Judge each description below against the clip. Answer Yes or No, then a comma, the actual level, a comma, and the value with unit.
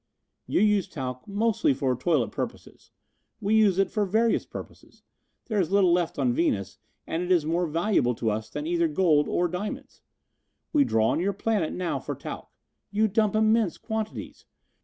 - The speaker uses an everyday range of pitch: No, wide, 5.8 semitones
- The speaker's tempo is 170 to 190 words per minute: Yes, average, 175 wpm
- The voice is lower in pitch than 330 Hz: Yes, medium, 185 Hz